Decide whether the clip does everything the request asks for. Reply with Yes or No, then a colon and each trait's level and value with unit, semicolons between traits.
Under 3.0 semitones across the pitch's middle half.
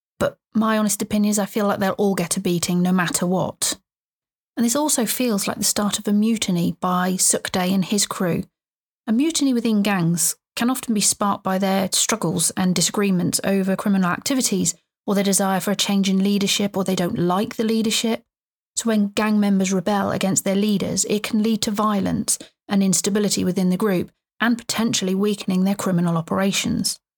Yes: narrow, 2.6 semitones